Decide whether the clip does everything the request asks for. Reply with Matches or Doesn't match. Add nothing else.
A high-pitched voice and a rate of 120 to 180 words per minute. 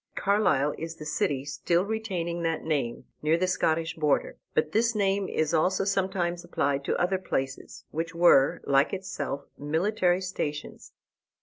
Doesn't match